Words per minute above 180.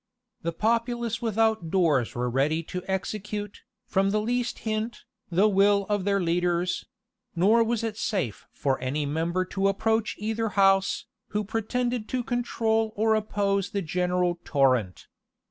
No: average, 145 wpm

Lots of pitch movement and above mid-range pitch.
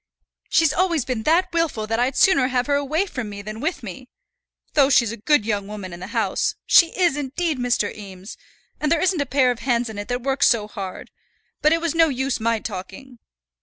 Yes: wide, 5.8 semitones; very high, 255 Hz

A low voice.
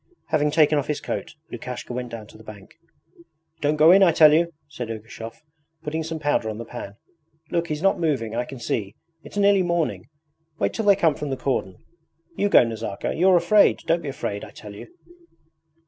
No: medium, 150 Hz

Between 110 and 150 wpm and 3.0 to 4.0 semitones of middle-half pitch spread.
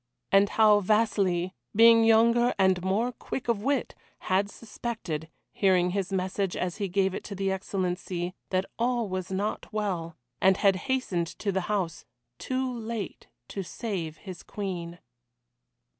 Yes: average, 145 wpm; average, 3.3 semitones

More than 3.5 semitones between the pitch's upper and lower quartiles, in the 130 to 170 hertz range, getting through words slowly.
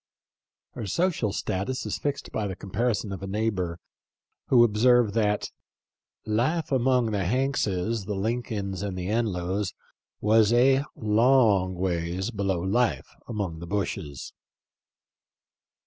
No: average, 3.9 semitones; low, 105 Hz; slow, 130 wpm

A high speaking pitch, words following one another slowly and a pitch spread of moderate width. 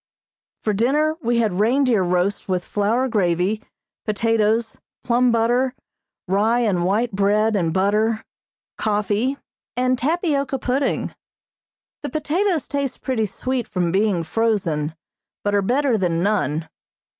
Yes: high, 220 Hz; slow, 120 wpm; average, 4.4 semitones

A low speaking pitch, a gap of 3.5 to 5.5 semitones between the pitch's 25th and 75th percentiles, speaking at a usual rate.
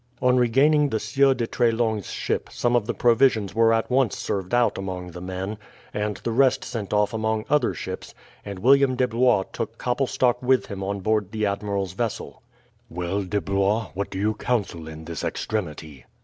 Yes: low, 110 Hz; average, 3.9 semitones; average, 185 wpm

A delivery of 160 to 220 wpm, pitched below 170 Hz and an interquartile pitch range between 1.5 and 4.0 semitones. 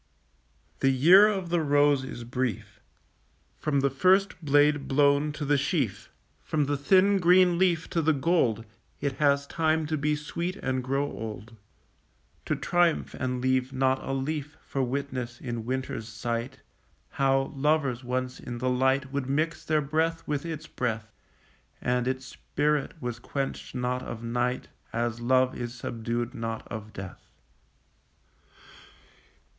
No: average, 145 wpm; low, 135 Hz; average, 3.5 semitones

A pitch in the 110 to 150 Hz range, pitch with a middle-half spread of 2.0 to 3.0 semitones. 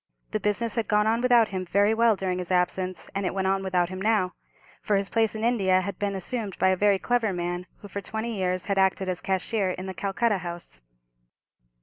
No: high, 195 Hz; average, 2.7 semitones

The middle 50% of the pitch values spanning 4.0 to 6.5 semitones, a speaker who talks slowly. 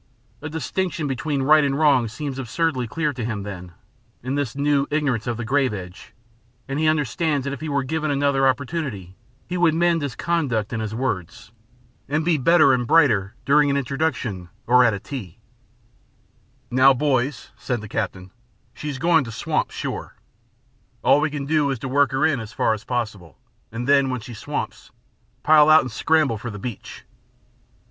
No: average, 4.6 semitones; average, 185 wpm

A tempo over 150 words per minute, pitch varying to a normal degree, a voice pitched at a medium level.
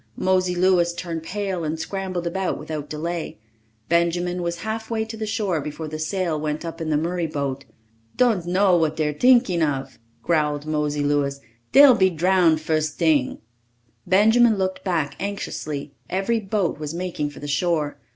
Yes: average, 160 wpm; average, 3.7 semitones; medium, 170 Hz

